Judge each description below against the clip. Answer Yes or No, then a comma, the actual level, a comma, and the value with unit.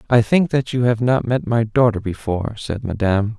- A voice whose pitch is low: Yes, low, 115 Hz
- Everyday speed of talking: No, fast, 210 wpm